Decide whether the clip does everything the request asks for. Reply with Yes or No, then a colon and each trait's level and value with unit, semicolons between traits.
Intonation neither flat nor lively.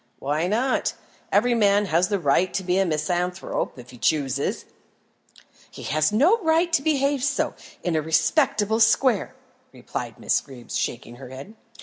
No: wide, 7.5 semitones